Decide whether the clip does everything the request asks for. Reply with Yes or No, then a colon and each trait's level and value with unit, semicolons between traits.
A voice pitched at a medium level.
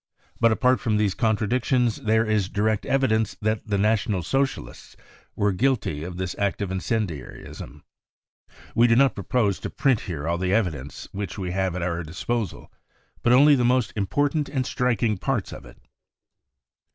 No: low, 105 Hz